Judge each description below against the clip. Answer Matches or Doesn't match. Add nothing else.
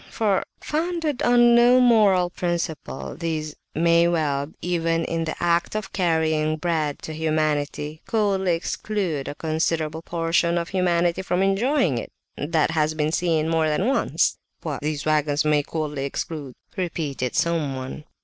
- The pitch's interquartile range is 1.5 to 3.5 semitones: Matches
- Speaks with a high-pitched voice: Doesn't match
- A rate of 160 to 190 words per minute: Doesn't match